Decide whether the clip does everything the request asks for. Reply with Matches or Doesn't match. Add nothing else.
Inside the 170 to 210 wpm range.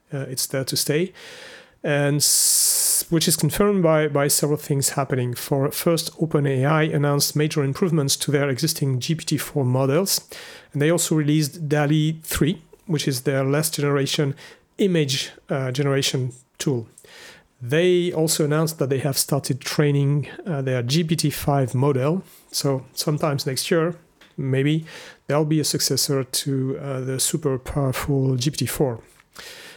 Doesn't match